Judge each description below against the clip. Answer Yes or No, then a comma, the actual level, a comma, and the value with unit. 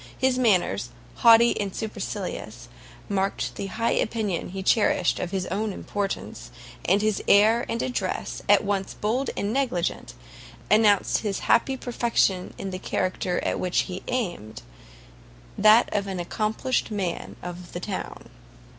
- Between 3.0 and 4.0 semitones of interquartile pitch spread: Yes, average, 3.7 semitones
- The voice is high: Yes, high, 200 Hz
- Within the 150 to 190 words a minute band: No, average, 140 wpm